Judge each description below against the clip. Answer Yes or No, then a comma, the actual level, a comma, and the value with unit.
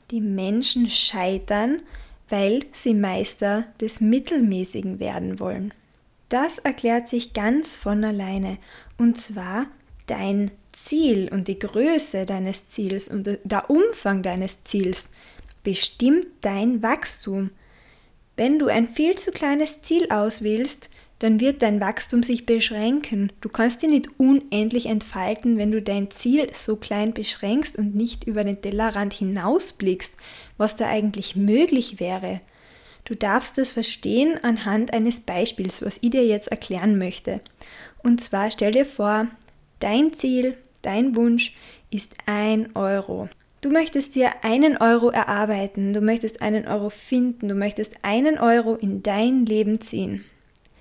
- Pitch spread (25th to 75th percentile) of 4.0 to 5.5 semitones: No, average, 3.5 semitones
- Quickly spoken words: No, average, 135 wpm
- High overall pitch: Yes, high, 220 Hz